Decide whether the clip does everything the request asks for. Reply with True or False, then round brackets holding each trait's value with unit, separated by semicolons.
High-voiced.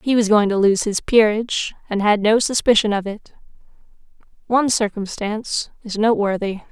True (215 Hz)